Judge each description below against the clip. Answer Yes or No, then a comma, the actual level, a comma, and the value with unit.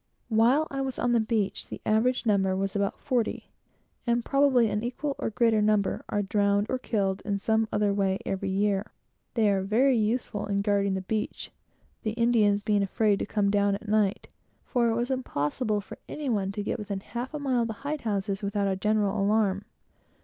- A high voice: Yes, high, 210 Hz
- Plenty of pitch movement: No, average, 2.9 semitones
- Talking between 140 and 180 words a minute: No, average, 200 wpm